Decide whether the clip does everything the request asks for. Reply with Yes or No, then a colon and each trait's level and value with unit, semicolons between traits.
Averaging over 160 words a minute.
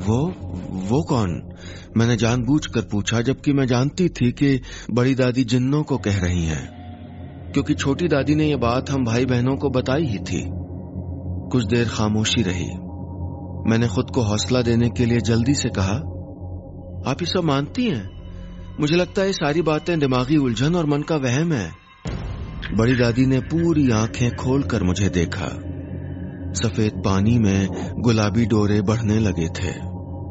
No: average, 155 wpm